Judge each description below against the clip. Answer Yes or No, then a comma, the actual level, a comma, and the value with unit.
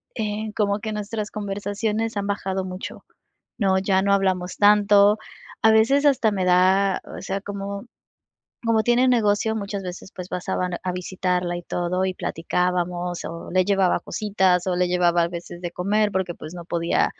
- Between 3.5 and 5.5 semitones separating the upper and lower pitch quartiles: No, narrow, 2.6 semitones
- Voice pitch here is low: No, high, 195 Hz